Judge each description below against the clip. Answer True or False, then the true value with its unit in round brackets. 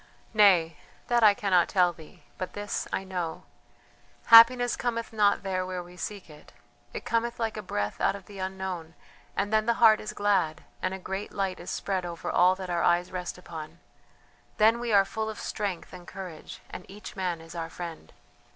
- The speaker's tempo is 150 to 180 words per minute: False (195 wpm)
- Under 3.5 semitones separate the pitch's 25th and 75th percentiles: True (3.1 semitones)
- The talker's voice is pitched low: False (190 Hz)